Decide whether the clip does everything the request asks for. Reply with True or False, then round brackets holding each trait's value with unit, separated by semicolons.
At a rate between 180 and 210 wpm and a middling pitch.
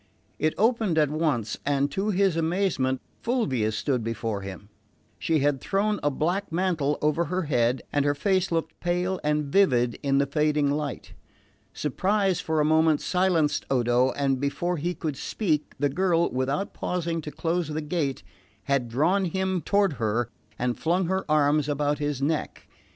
False (165 wpm; 150 Hz)